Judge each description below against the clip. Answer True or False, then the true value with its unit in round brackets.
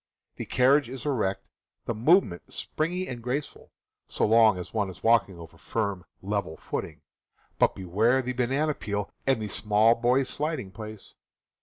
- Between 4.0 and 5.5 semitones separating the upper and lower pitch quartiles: True (4.5 semitones)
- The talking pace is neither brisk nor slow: True (160 wpm)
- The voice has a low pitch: True (115 Hz)